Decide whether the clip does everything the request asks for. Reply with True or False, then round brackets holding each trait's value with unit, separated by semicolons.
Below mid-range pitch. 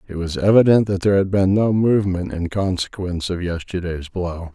True (95 Hz)